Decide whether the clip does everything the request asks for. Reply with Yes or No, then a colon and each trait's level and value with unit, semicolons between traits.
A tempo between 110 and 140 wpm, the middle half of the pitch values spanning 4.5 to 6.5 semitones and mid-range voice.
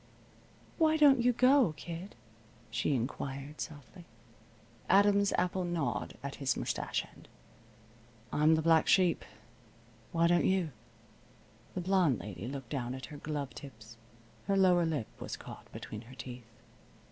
Yes: slow, 135 wpm; wide, 5.6 semitones; medium, 160 Hz